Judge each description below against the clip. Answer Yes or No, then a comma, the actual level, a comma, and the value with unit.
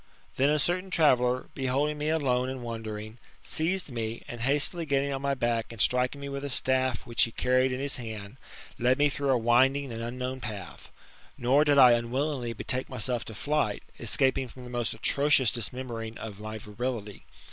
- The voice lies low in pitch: Yes, low, 125 Hz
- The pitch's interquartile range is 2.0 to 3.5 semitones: Yes, average, 3.1 semitones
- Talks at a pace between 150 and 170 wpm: No, average, 185 wpm